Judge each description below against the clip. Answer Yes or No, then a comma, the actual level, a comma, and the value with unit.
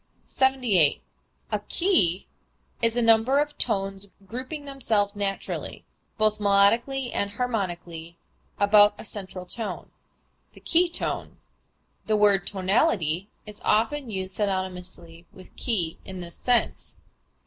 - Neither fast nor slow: No, slow, 115 wpm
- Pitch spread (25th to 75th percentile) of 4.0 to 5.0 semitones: Yes, average, 4.3 semitones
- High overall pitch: Yes, high, 205 Hz